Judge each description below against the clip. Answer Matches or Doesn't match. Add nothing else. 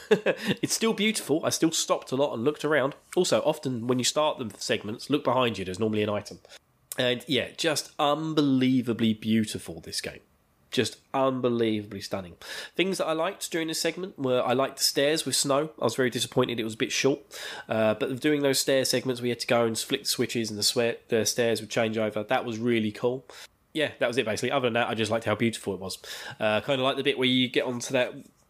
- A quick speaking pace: Matches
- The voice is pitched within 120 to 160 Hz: Matches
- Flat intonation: Doesn't match